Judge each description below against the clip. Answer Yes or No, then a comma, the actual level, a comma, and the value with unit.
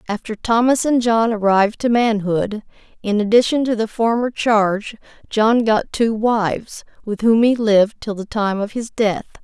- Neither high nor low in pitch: No, high, 220 Hz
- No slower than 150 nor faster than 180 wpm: Yes, average, 170 wpm